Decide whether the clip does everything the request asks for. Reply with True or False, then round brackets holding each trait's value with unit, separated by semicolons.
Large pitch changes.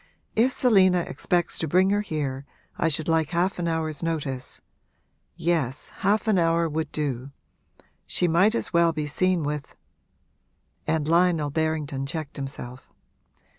False (3.2 semitones)